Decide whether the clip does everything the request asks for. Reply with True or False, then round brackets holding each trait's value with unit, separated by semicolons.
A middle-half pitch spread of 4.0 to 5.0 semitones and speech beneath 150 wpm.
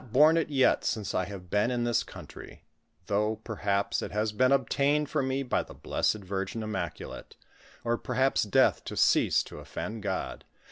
False (4.5 semitones; 185 wpm)